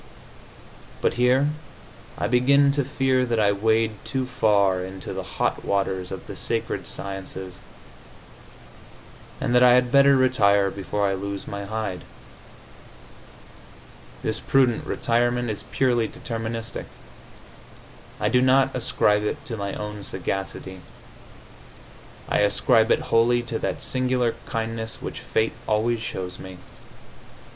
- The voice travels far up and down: No, average, 3.8 semitones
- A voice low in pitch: Yes, low, 115 Hz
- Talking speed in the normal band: No, slow, 125 wpm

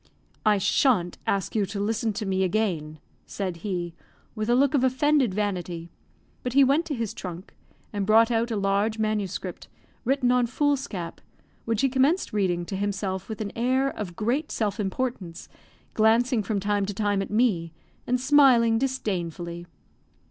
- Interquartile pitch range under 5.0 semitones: Yes, average, 4.5 semitones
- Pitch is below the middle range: No, high, 215 Hz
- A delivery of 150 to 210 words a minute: Yes, average, 160 wpm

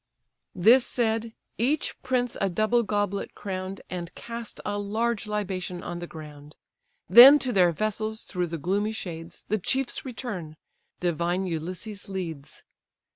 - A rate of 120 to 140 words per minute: Yes, slow, 135 wpm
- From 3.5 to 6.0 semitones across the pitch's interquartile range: Yes, average, 4.4 semitones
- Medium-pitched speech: No, high, 200 Hz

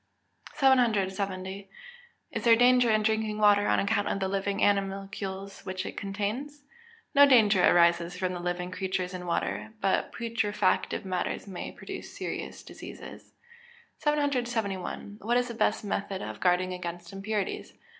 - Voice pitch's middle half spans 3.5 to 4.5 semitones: No, average, 3.0 semitones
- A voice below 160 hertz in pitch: No, high, 200 Hz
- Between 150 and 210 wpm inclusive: No, average, 140 wpm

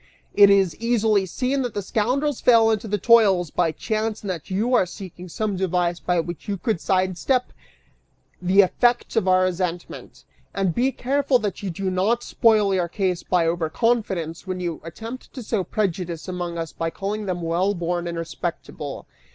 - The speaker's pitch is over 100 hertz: Yes, high, 190 Hz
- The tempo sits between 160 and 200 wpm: Yes, average, 180 wpm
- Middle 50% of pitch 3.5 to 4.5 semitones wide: Yes, average, 4.1 semitones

